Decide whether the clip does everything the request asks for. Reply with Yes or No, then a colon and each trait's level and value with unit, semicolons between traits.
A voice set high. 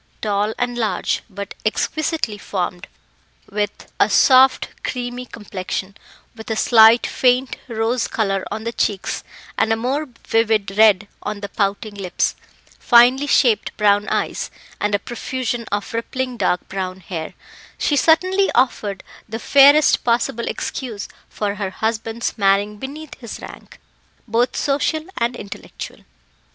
Yes: high, 225 Hz